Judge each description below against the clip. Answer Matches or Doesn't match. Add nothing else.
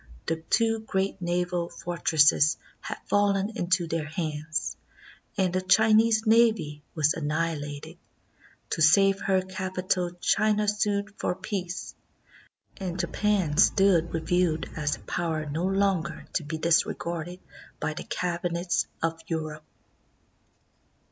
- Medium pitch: Matches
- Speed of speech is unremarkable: Doesn't match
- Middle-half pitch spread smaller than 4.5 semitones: Matches